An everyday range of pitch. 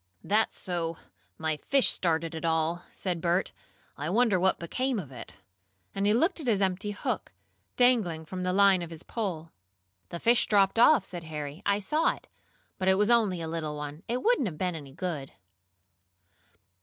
Yes: average, 4.4 semitones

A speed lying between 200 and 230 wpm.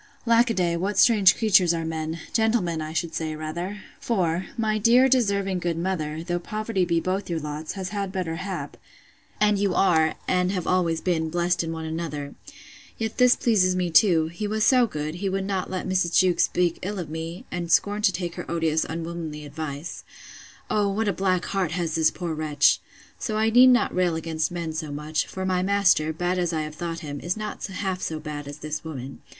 Yes: fast, 205 wpm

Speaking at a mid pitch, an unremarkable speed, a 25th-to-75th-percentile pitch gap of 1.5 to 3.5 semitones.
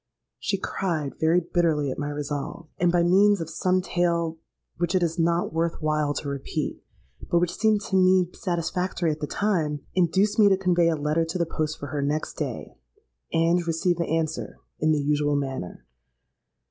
Yes: medium, 165 Hz; average, 185 wpm; average, 2.8 semitones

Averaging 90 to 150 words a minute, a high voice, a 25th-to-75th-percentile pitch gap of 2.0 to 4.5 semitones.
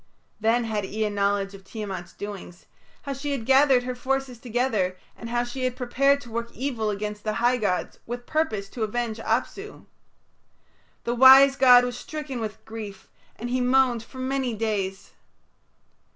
No: average, 165 wpm; high, 240 Hz; average, 3.6 semitones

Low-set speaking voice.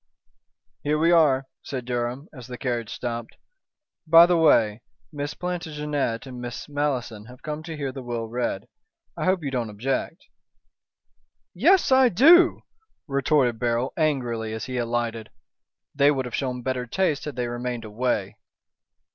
Yes: low, 130 Hz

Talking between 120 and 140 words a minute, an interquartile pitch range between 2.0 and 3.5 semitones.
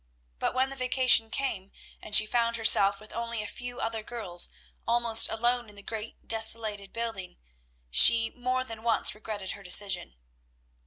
No: average, 160 wpm; narrow, 2.4 semitones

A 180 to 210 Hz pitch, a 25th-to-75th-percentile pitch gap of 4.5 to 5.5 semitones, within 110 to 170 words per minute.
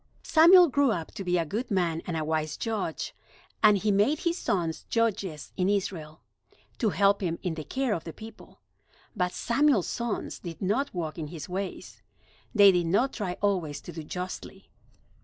No: high, 190 Hz; average, 5.1 semitones; average, 180 wpm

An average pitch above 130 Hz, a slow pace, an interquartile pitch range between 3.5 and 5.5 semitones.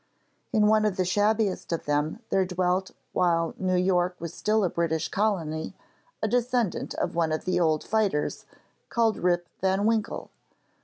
No: medium, 185 Hz; average, 160 wpm; average, 3.9 semitones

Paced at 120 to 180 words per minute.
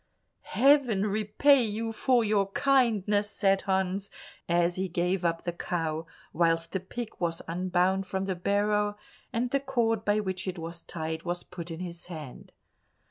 Yes: average, 160 wpm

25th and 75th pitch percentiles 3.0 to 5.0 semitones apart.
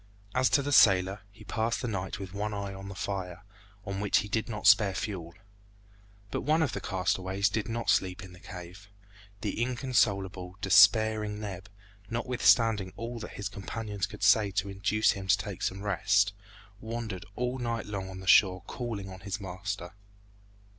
No: narrow, 2.6 semitones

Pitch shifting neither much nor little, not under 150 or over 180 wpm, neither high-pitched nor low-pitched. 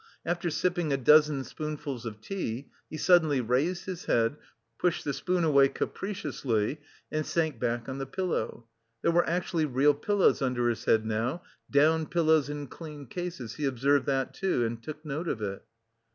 Yes: average, 4.9 semitones; average, 170 wpm; medium, 145 Hz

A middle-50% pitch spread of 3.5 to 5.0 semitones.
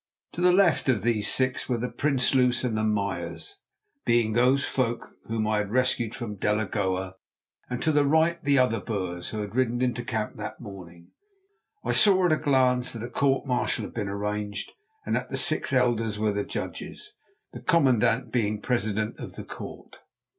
Yes: average, 3.8 semitones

